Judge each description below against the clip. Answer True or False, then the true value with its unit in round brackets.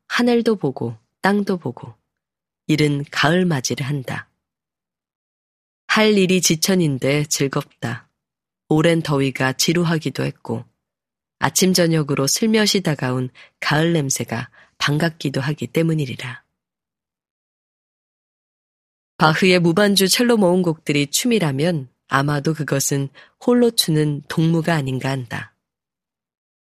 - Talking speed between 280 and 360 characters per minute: False (230 characters per minute)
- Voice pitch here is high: False (150 Hz)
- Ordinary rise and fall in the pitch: True (4.4 semitones)